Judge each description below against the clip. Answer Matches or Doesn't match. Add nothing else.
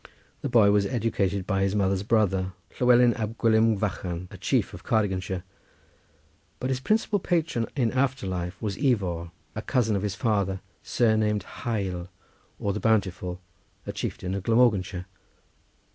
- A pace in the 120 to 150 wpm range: Matches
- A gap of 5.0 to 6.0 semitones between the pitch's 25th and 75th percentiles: Doesn't match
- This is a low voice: Matches